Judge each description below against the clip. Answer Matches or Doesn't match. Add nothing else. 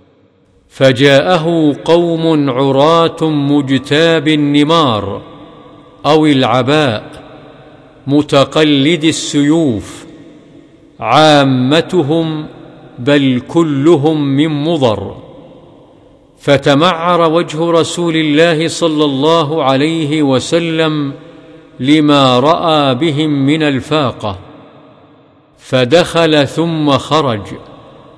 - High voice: Doesn't match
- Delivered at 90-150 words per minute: Doesn't match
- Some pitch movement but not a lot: Doesn't match